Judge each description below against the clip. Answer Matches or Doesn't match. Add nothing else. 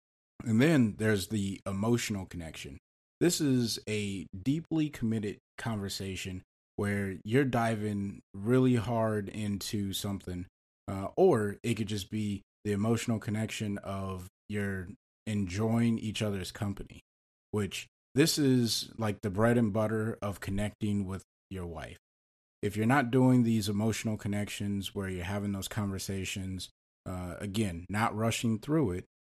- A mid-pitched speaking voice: Doesn't match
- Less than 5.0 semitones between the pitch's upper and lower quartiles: Matches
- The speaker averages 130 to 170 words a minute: Matches